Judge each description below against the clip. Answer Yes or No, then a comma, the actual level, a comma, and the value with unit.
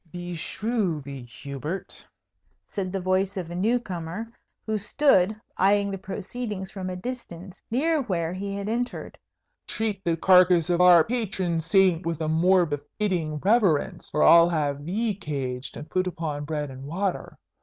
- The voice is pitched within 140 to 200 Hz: Yes, medium, 185 Hz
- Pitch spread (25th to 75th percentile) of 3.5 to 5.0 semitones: Yes, average, 3.8 semitones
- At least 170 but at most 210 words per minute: No, average, 155 wpm